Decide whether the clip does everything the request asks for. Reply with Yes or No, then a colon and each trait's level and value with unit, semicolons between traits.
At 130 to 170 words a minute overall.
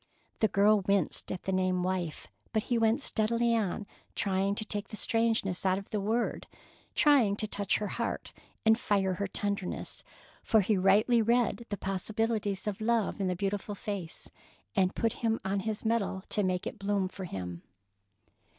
No: average, 180 wpm